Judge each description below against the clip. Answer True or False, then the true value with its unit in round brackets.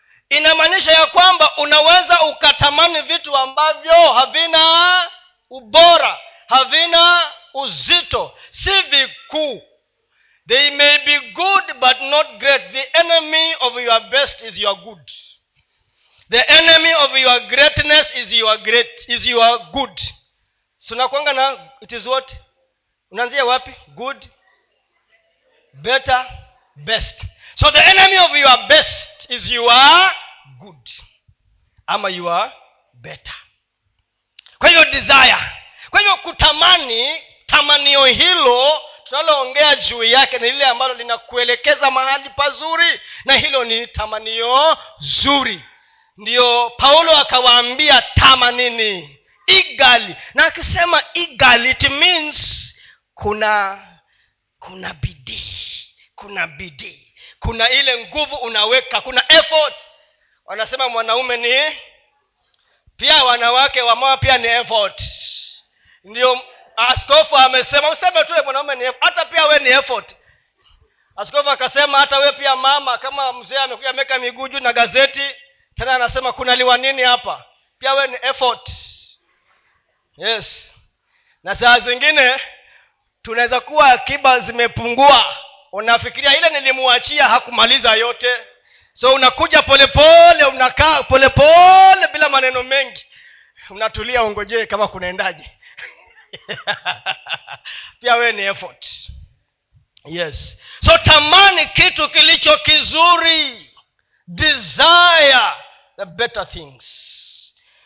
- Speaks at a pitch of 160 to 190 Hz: False (270 Hz)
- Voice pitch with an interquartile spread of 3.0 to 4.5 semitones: True (4.0 semitones)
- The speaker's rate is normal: False (95 wpm)